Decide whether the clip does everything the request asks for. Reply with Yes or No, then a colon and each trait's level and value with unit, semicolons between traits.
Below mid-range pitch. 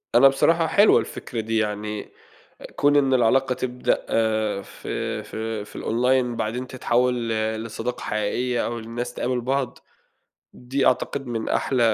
Yes: low, 120 Hz